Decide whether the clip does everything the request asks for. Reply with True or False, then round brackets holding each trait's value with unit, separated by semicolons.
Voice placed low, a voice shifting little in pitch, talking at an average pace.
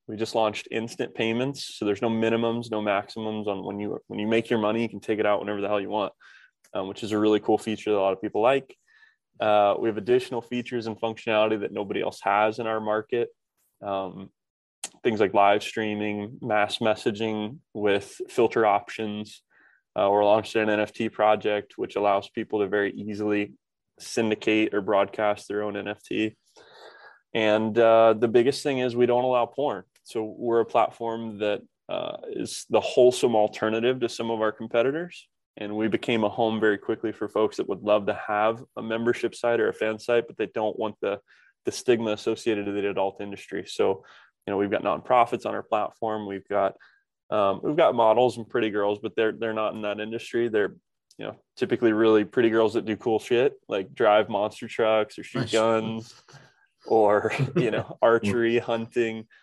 True (110 Hz; 1.7 semitones; 195 wpm)